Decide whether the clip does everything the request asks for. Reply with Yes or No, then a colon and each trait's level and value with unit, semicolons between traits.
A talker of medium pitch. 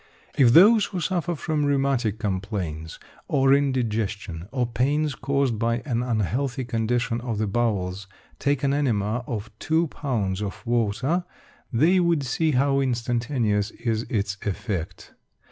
No: low, 120 Hz